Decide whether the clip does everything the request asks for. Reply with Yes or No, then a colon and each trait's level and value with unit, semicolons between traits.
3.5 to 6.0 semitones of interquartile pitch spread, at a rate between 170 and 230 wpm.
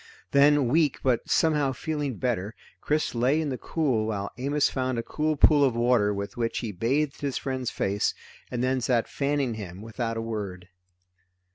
Yes: average, 4.1 semitones; average, 175 wpm